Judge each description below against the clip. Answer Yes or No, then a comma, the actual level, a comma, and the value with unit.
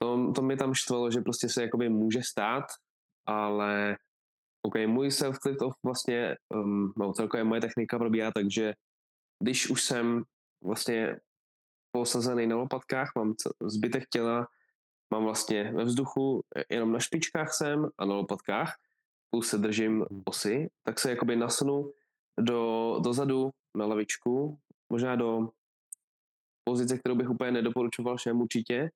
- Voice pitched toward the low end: Yes, low, 120 Hz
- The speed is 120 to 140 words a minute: Yes, average, 135 wpm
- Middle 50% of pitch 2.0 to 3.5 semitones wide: Yes, narrow, 2.5 semitones